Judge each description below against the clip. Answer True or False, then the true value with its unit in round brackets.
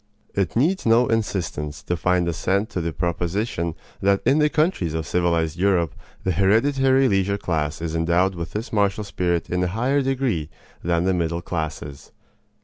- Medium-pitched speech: False (90 Hz)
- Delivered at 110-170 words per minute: True (165 wpm)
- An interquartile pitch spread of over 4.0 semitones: True (4.7 semitones)